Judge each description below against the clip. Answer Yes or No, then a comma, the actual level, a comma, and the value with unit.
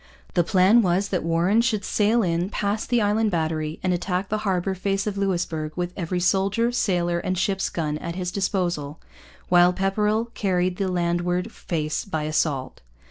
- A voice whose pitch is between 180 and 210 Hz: Yes, medium, 185 Hz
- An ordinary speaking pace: Yes, average, 170 wpm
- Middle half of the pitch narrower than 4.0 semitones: Yes, average, 2.7 semitones